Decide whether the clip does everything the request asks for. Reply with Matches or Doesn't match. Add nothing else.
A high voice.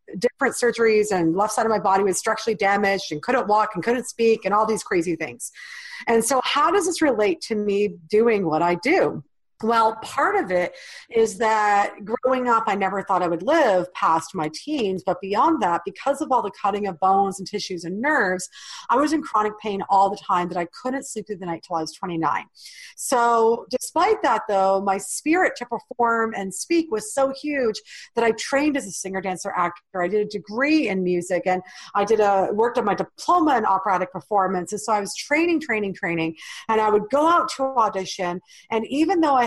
Matches